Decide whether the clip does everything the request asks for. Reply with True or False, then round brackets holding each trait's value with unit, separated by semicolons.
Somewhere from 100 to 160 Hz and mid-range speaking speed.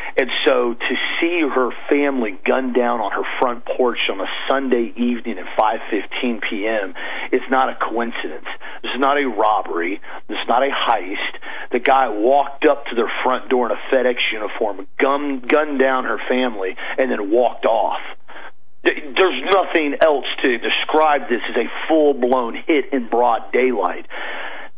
True (135 Hz; 160 wpm)